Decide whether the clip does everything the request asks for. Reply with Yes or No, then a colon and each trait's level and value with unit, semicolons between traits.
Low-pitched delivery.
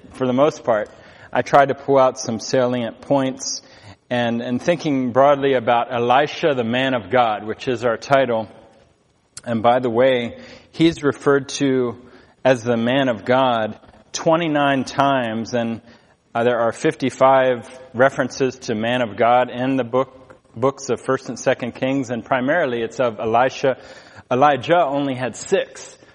Yes: low, 130 Hz